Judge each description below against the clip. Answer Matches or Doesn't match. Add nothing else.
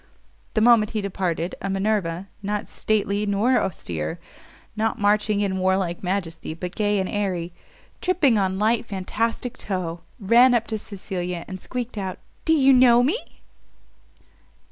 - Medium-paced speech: Matches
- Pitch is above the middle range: Matches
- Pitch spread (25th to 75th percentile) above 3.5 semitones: Doesn't match